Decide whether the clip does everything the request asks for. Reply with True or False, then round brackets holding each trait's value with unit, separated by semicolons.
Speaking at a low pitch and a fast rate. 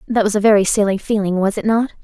False (210 Hz; 265 wpm)